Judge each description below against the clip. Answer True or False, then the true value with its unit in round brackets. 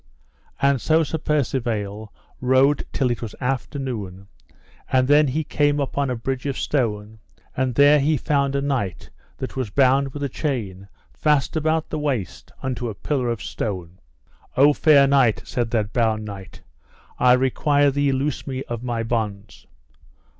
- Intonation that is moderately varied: True (4.0 semitones)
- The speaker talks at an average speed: True (160 wpm)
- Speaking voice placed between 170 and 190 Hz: False (130 Hz)